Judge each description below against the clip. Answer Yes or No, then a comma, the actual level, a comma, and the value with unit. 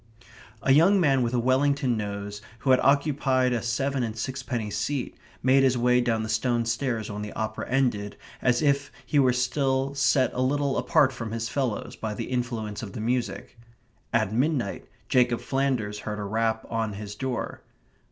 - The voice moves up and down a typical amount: Yes, average, 3.4 semitones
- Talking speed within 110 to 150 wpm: No, average, 180 wpm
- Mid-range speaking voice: No, low, 125 Hz